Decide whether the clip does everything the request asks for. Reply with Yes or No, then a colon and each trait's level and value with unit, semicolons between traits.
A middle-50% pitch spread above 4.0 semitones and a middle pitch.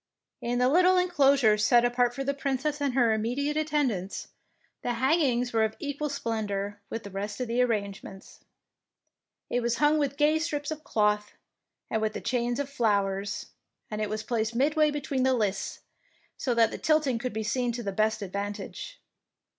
No: average, 4.7 semitones; high, 245 Hz